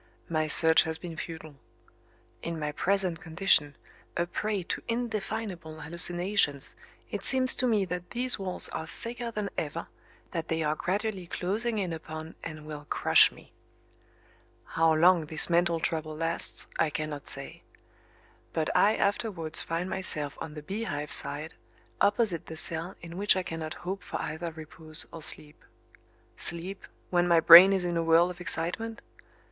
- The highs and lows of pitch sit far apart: No, average, 3.5 semitones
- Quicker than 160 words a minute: No, average, 155 wpm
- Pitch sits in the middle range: Yes, medium, 170 Hz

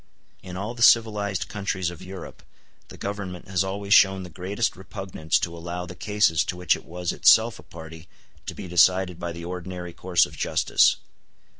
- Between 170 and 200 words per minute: Yes, average, 180 wpm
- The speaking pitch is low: Yes, very low, 90 Hz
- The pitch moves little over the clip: Yes, narrow, 2.3 semitones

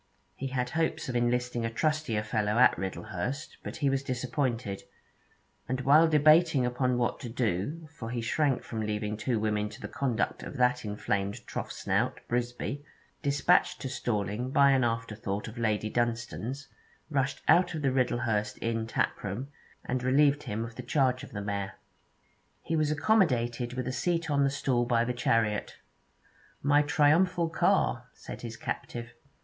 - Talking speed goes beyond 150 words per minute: Yes, average, 160 wpm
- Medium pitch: No, low, 125 Hz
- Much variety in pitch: No, average, 3.7 semitones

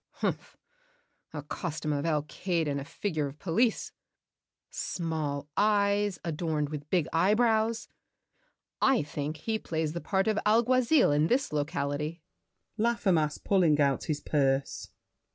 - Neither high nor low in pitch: Yes, medium, 165 Hz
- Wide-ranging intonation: Yes, wide, 5.8 semitones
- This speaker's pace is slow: Yes, slow, 130 wpm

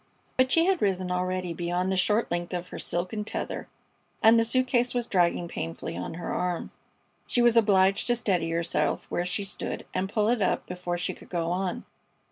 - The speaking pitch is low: No, medium, 185 Hz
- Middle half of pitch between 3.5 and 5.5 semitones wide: Yes, average, 4.3 semitones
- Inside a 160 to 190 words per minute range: No, average, 200 wpm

